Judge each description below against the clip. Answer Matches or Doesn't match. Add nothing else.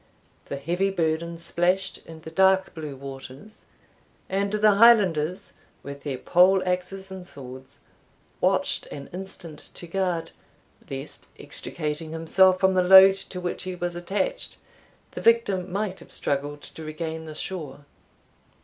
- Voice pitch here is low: Doesn't match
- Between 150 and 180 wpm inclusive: Doesn't match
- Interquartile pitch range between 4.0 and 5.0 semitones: Doesn't match